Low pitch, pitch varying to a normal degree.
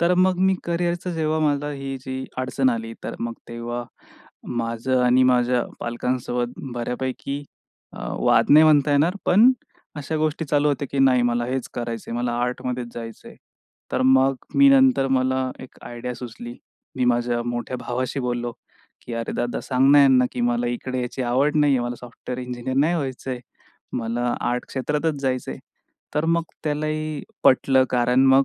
Yes: low, 130 Hz; average, 3.2 semitones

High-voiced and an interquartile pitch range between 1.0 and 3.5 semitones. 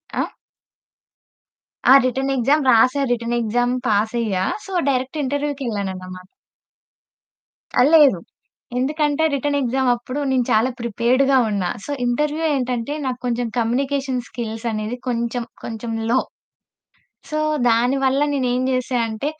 Yes: high, 245 Hz; average, 2.7 semitones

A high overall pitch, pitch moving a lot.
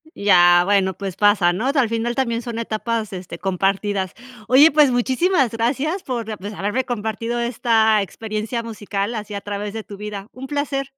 No: high, 220 Hz; average, 3.3 semitones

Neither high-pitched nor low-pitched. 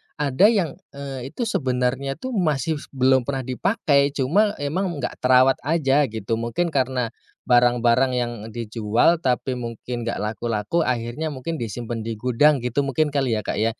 No: low, 130 Hz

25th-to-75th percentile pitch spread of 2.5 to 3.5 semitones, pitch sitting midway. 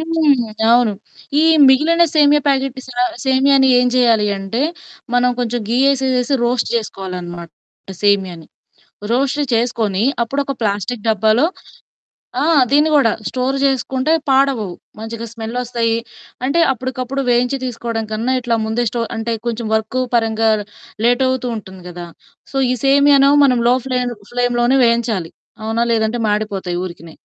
No: average, 3.2 semitones; high, 240 Hz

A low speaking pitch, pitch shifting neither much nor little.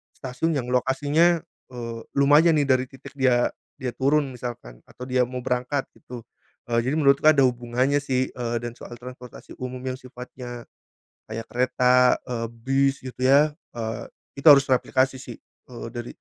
No: low, 130 Hz; narrow, 2.1 semitones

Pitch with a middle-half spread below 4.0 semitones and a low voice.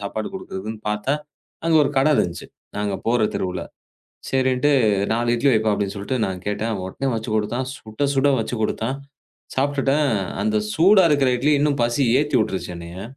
No: average, 4.7 semitones; low, 120 Hz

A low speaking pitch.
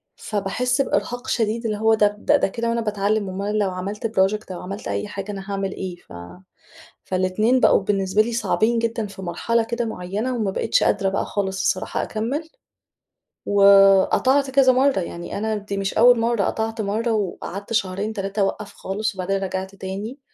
No: high, 210 Hz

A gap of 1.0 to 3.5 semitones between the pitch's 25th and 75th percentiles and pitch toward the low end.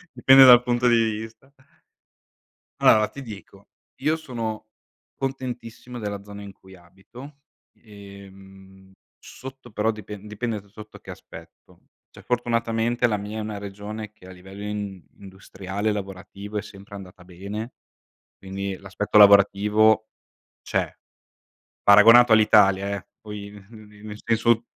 Yes: narrow, 2.6 semitones; low, 105 Hz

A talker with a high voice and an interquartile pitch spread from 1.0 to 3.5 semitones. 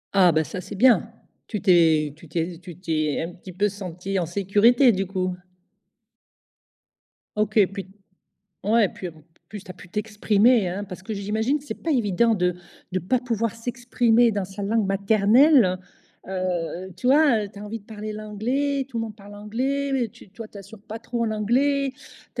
No: high, 205 Hz; average, 3.9 semitones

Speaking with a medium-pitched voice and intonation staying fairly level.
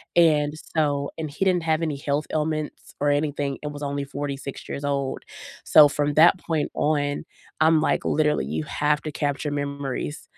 Yes: medium, 145 Hz; narrow, 1.5 semitones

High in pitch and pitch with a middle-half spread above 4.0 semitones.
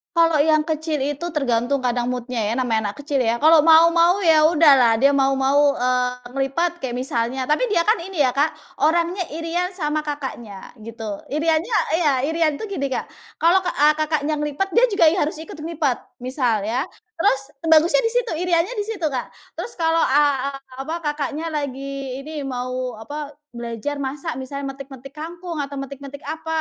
No: very high, 290 Hz; average, 3.7 semitones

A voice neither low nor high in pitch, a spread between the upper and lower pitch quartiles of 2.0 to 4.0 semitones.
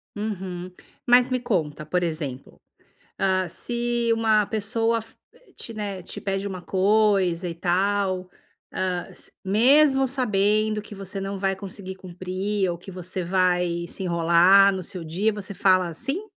No: high, 195 Hz; average, 2.9 semitones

